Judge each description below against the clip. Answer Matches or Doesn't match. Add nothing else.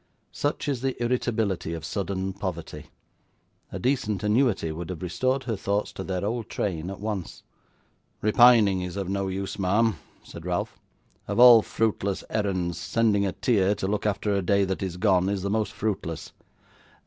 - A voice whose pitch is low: Matches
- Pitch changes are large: Doesn't match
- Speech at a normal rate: Matches